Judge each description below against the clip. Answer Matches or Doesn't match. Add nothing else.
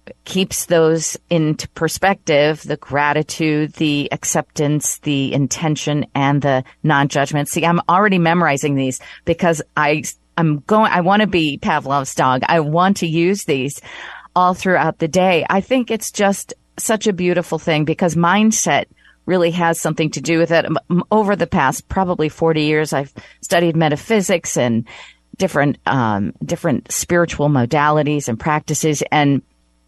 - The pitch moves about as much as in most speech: Matches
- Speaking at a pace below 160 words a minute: Matches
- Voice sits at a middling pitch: Matches